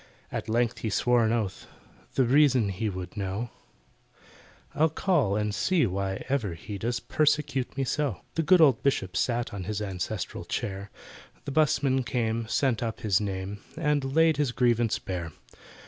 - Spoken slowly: No, average, 165 wpm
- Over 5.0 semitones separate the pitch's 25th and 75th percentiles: Yes, wide, 5.5 semitones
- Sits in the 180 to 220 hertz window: No, low, 115 Hz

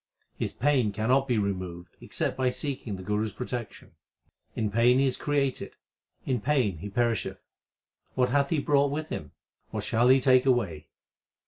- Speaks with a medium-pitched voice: No, low, 125 Hz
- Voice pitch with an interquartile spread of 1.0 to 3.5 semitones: No, average, 4.6 semitones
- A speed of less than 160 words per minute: No, average, 165 wpm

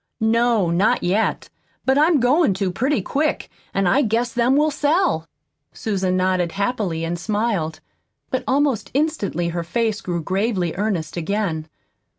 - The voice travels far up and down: Yes, wide, 6.1 semitones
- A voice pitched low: No, high, 210 Hz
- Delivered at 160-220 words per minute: No, average, 145 wpm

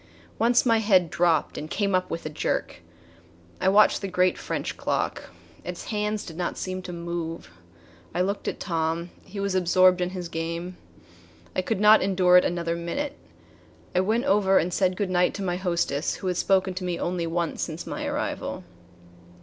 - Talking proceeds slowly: No, average, 185 wpm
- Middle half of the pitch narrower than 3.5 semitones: Yes, narrow, 2.4 semitones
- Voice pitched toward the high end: No, medium, 180 Hz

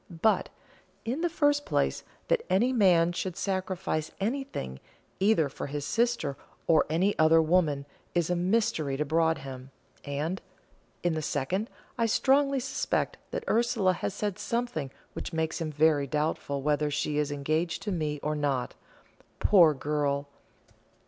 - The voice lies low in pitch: No, medium, 165 Hz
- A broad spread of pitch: Yes, wide, 5.7 semitones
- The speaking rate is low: No, average, 145 wpm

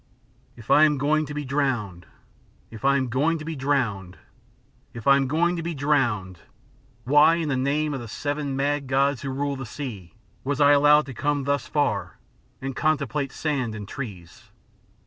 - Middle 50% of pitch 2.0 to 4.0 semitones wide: Yes, average, 2.9 semitones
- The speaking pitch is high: No, medium, 140 Hz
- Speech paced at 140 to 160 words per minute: No, average, 185 wpm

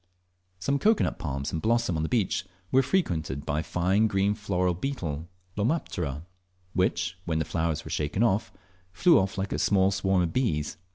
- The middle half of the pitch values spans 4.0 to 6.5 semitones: Yes, average, 5.2 semitones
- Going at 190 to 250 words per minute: No, average, 175 wpm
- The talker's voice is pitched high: No, very low, 95 Hz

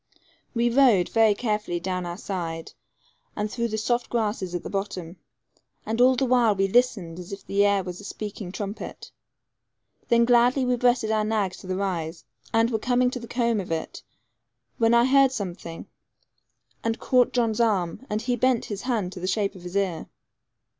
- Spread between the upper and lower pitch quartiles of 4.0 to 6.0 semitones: Yes, average, 4.3 semitones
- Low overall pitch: No, high, 215 Hz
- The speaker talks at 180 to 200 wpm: Yes, average, 190 wpm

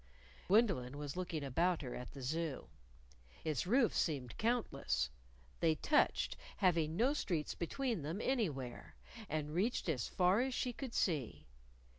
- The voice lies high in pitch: No, medium, 165 Hz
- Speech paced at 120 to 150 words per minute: Yes, average, 140 wpm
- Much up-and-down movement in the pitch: Yes, wide, 7.5 semitones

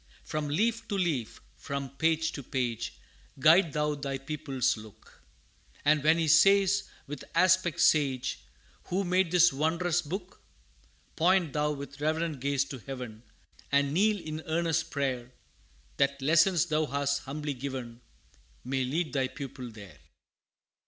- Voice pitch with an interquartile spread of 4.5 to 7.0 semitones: No, average, 3.9 semitones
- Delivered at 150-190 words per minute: No, average, 140 wpm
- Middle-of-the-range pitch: Yes, medium, 150 Hz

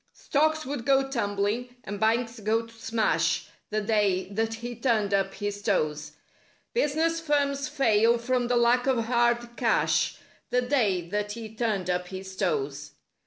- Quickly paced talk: No, average, 155 wpm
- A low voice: No, high, 225 Hz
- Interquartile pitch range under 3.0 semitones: No, average, 3.5 semitones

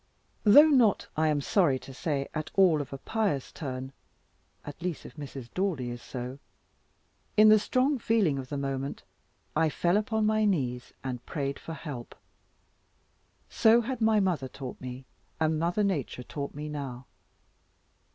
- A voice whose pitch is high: No, medium, 155 Hz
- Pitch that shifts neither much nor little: No, wide, 7.3 semitones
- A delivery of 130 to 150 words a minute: No, average, 160 wpm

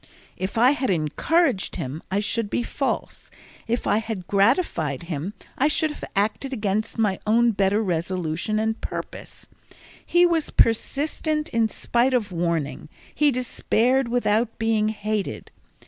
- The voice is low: No, high, 220 Hz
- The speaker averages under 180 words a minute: Yes, average, 140 wpm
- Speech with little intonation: No, average, 4.6 semitones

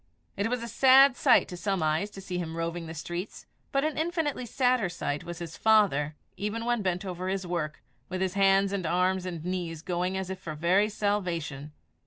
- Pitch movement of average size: Yes, average, 3.5 semitones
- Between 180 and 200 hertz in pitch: Yes, medium, 185 Hz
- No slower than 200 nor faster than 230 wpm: Yes, fast, 205 wpm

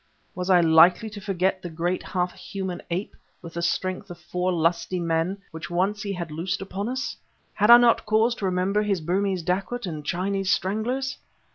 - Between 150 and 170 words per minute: No, average, 185 wpm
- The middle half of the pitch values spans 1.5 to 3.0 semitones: Yes, average, 2.7 semitones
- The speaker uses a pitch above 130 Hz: Yes, medium, 185 Hz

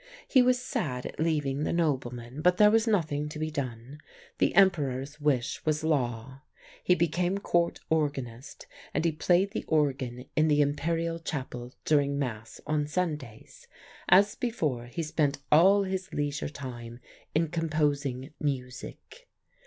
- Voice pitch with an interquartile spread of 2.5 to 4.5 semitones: Yes, average, 4.0 semitones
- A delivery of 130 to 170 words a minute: Yes, average, 145 wpm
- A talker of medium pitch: Yes, medium, 150 Hz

